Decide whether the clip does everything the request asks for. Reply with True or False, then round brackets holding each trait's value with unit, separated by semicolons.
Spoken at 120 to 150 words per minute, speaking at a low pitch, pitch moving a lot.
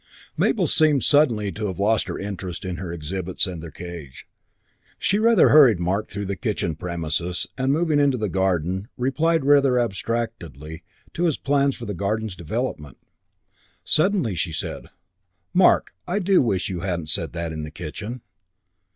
False (160 wpm; 100 Hz; 7.7 semitones)